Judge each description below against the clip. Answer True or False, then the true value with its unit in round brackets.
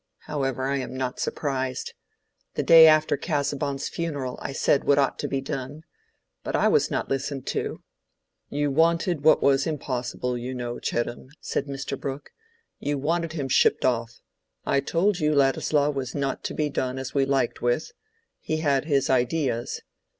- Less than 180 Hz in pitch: True (140 Hz)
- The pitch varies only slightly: True (2.3 semitones)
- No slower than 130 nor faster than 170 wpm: True (165 wpm)